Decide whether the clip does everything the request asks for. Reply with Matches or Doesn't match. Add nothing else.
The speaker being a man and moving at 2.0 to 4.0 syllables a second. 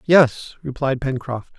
Matches